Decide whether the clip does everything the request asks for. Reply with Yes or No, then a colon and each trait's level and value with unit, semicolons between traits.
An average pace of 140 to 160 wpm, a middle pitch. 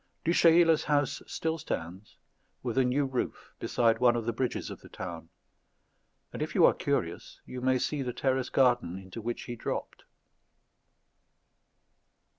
No: average, 155 wpm; low, 125 Hz